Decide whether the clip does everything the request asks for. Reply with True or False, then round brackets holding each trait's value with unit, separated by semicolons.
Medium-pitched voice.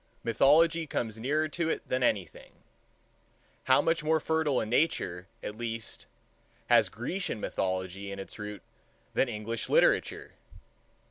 False (120 Hz)